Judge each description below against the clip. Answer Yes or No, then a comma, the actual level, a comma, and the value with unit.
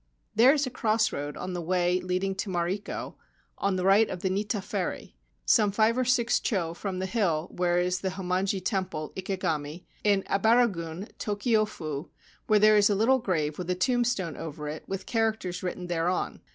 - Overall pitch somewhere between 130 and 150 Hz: No, high, 190 Hz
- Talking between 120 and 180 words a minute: No, average, 190 wpm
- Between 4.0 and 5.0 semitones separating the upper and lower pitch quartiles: No, average, 3.3 semitones